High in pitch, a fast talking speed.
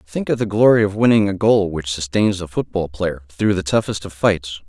No: very low, 95 Hz; fast, 230 wpm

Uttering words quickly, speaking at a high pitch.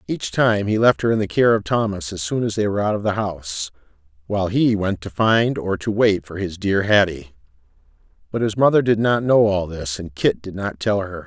No: fast, 240 wpm; low, 110 Hz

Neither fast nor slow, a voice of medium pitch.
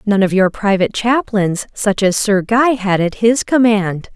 No: average, 190 wpm; high, 210 Hz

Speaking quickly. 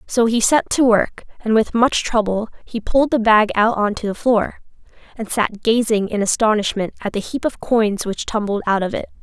Yes: fast, 215 wpm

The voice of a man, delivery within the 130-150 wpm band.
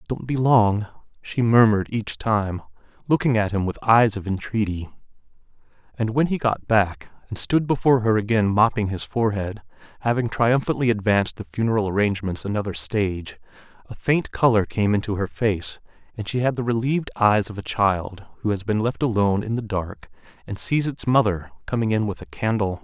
No: male; average, 180 wpm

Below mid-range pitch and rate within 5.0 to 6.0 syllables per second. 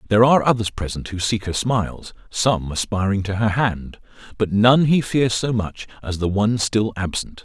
Yes: low, 105 Hz; 5.1 syllables/s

